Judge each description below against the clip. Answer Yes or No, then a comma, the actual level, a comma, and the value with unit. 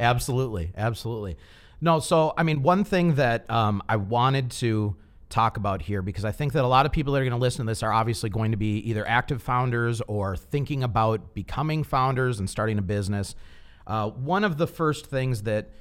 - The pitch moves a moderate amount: Yes, average, 4.3 semitones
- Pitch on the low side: Yes, low, 115 Hz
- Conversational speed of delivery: No, fast, 210 wpm